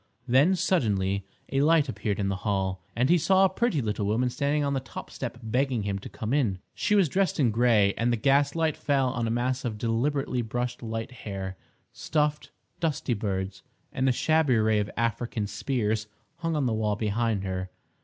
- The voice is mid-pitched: No, low, 120 Hz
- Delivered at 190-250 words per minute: Yes, average, 195 wpm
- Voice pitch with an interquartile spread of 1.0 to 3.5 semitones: No, average, 5.0 semitones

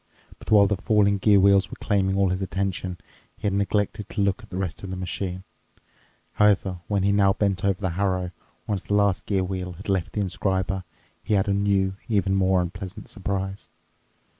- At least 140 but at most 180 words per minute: No, average, 195 wpm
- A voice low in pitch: Yes, very low, 95 Hz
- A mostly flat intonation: Yes, narrow, 1.3 semitones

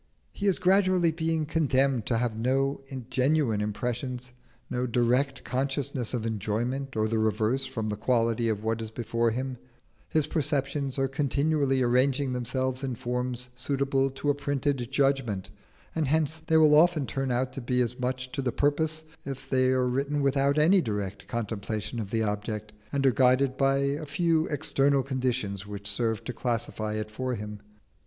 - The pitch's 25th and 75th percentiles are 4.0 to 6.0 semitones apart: No, average, 3.3 semitones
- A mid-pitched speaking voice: No, low, 130 Hz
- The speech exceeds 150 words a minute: Yes, average, 170 wpm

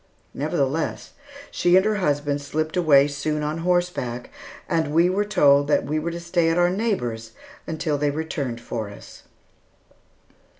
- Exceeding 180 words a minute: No, average, 155 wpm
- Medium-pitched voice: Yes, medium, 155 Hz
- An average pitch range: Yes, average, 3.5 semitones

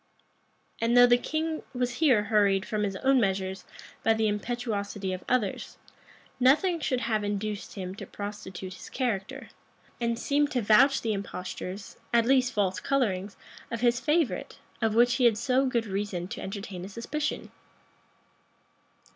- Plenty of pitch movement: No, average, 3.9 semitones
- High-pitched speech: Yes, high, 225 Hz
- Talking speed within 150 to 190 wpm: Yes, average, 155 wpm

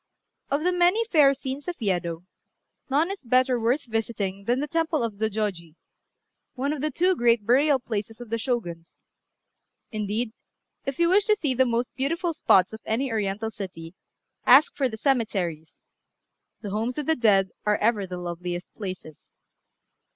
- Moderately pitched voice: No, high, 235 Hz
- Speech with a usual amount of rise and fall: No, wide, 5.7 semitones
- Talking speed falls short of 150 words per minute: No, average, 165 wpm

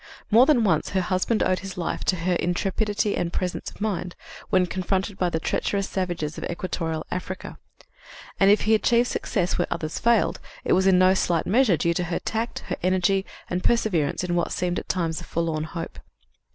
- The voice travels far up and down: No, narrow, 2.6 semitones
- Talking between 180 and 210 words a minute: Yes, average, 195 wpm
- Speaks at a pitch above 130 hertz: Yes, medium, 185 Hz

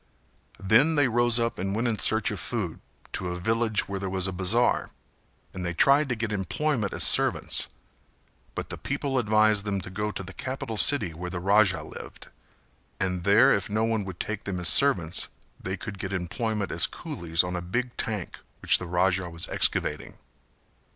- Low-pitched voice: Yes, low, 100 Hz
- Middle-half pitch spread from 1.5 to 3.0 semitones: No, average, 3.8 semitones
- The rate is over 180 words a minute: Yes, average, 190 wpm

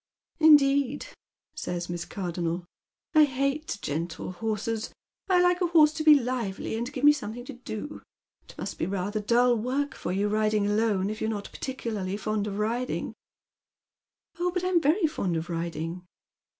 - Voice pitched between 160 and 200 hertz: No, high, 225 Hz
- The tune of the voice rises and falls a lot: Yes, wide, 6.5 semitones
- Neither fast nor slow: Yes, average, 170 wpm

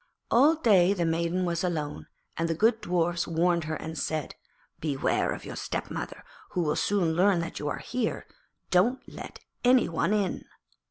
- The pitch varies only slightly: No, average, 3.8 semitones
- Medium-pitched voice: Yes, medium, 175 Hz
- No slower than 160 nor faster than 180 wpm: Yes, average, 170 wpm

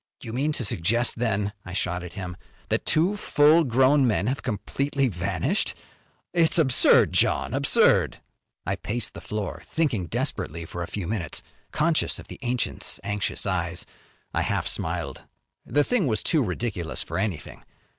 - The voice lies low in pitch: Yes, low, 115 Hz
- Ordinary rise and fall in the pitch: No, wide, 7.0 semitones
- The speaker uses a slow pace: No, average, 155 wpm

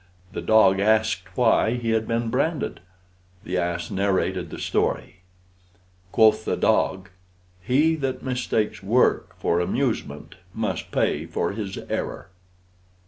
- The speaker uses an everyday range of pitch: Yes, average, 4.1 semitones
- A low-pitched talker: Yes, low, 110 Hz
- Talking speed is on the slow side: Yes, slow, 125 wpm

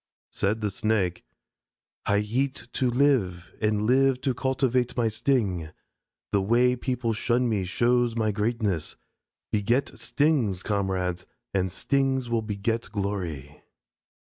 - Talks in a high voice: No, low, 110 Hz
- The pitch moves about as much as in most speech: Yes, average, 4.1 semitones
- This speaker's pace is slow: Yes, slow, 120 wpm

